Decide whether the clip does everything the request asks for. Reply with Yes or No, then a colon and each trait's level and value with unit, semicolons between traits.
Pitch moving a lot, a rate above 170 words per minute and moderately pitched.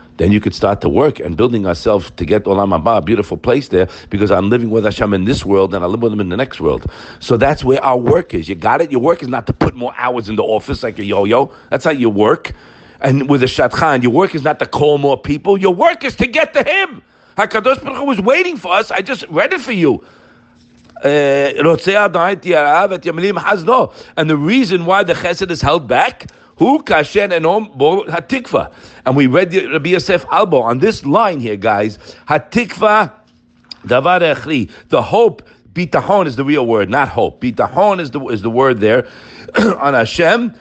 Yes: wide, 7.7 semitones; average, 200 wpm; medium, 165 Hz